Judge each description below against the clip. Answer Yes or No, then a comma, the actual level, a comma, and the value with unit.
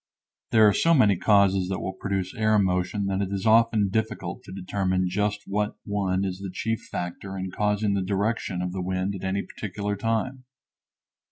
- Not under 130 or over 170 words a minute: No, average, 185 wpm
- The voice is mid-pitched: No, low, 100 Hz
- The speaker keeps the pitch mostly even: Yes, narrow, 2.0 semitones